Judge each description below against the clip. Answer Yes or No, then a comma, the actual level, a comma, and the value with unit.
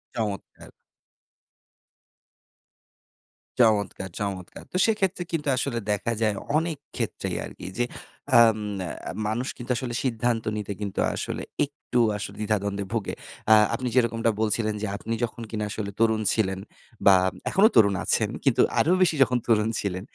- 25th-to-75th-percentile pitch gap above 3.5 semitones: No, average, 3.2 semitones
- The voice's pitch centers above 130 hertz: No, low, 110 Hz